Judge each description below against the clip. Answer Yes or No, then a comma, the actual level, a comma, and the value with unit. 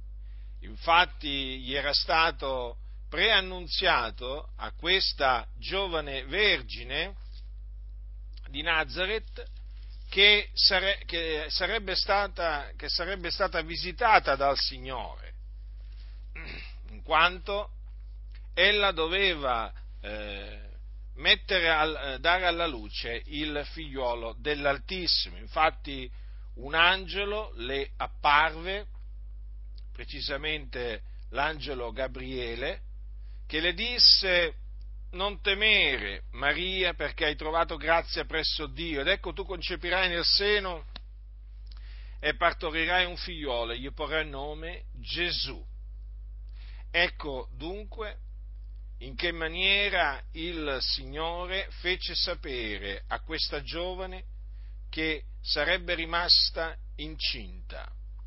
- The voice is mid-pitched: Yes, medium, 150 Hz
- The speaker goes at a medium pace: No, slow, 80 wpm